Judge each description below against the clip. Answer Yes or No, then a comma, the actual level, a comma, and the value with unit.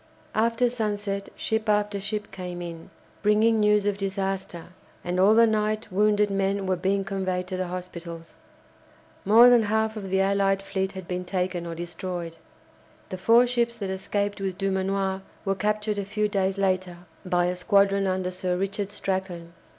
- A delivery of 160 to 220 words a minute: Yes, average, 165 wpm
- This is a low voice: No, high, 195 Hz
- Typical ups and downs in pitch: No, narrow, 2.2 semitones